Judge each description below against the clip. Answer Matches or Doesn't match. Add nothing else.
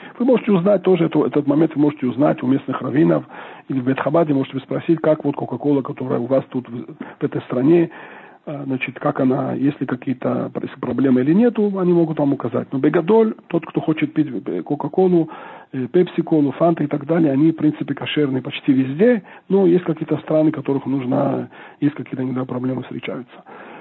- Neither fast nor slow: Doesn't match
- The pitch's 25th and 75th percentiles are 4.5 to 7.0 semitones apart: Doesn't match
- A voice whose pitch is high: Doesn't match